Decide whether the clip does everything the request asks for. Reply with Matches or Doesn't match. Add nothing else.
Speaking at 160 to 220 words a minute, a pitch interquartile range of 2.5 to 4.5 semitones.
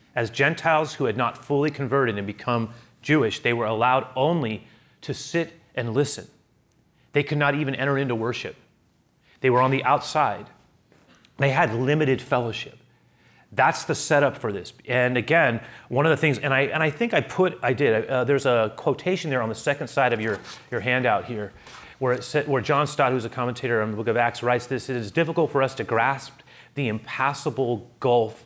Matches